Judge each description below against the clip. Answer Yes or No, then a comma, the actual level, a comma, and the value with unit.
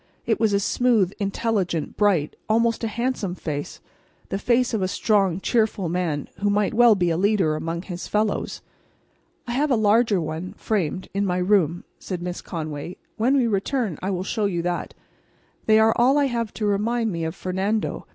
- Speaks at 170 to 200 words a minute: Yes, average, 180 wpm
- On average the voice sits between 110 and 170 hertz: No, high, 200 Hz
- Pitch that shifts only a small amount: No, average, 4.0 semitones